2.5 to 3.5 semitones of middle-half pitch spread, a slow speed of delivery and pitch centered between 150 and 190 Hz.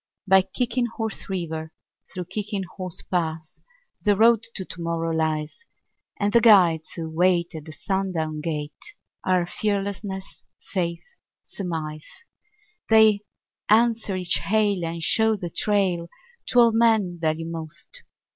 No: average, 4.3 semitones; slow, 125 wpm; medium, 185 Hz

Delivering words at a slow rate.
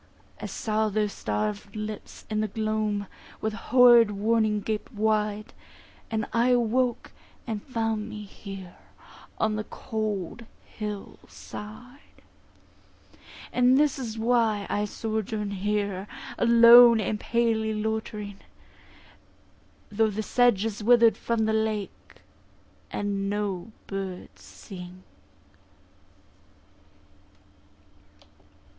Yes: slow, 100 wpm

